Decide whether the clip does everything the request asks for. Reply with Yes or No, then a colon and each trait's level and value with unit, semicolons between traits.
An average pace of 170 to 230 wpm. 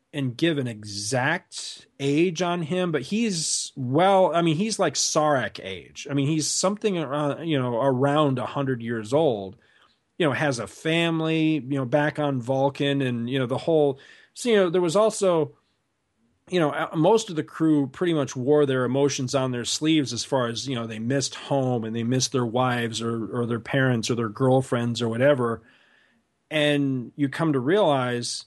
Yes: average, 190 wpm